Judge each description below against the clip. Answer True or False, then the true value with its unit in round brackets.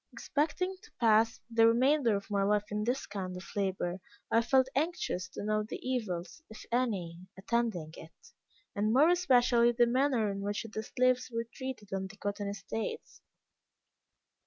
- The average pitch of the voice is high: True (220 Hz)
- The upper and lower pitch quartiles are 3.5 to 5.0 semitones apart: True (4.1 semitones)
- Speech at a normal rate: True (160 wpm)